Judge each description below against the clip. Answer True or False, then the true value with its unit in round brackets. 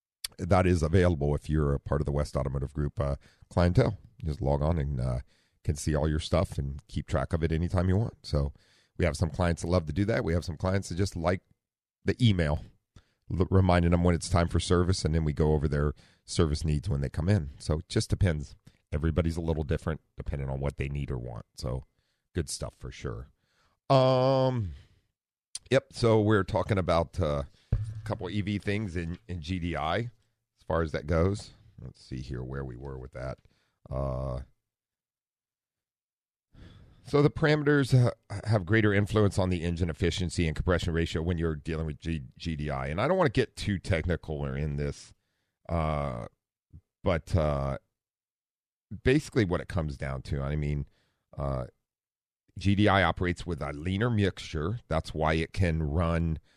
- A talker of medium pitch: False (85 Hz)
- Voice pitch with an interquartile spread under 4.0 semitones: False (5.1 semitones)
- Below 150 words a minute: False (185 wpm)